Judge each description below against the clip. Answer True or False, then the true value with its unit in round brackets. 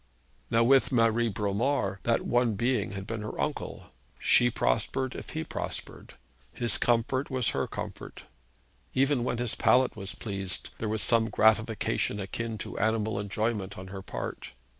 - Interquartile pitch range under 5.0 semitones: True (3.1 semitones)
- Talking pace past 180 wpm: False (155 wpm)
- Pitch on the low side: True (115 Hz)